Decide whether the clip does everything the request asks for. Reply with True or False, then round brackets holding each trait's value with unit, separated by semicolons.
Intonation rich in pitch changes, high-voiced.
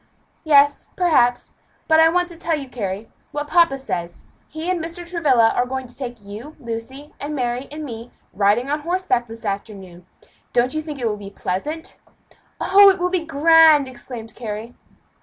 True (5.9 semitones; 270 Hz)